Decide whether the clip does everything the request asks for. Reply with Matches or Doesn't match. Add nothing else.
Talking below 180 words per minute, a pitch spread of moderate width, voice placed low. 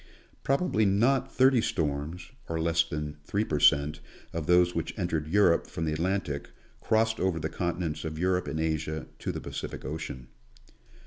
Matches